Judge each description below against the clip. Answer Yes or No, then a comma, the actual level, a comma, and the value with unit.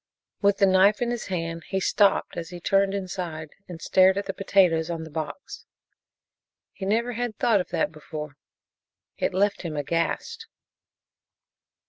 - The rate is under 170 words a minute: Yes, average, 155 wpm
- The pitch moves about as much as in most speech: Yes, average, 3.4 semitones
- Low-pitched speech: No, medium, 185 Hz